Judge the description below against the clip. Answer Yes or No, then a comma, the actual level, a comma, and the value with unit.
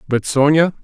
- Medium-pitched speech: Yes, medium, 145 Hz